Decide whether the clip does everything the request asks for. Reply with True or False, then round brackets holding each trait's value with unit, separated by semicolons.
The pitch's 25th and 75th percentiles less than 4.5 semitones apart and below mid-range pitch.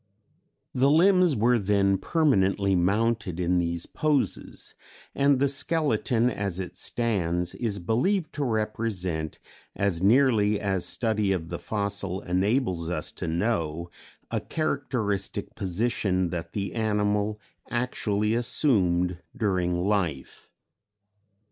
False (4.8 semitones; 105 Hz)